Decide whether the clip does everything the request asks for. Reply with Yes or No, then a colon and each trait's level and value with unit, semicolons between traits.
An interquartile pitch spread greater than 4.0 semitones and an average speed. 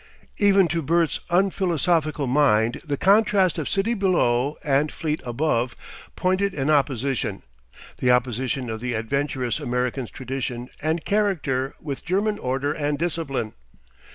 No: wide, 5.4 semitones; slow, 125 wpm